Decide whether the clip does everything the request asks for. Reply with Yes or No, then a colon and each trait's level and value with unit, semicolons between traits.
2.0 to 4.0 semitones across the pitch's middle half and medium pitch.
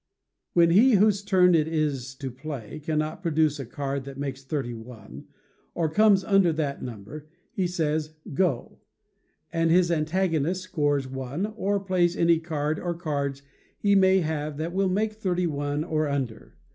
No: average, 4.4 semitones; medium, 155 Hz